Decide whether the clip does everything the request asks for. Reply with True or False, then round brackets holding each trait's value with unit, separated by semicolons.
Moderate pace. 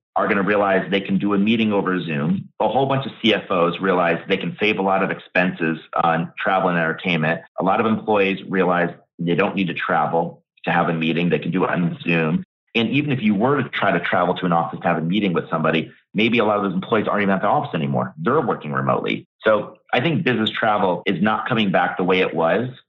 False (245 wpm)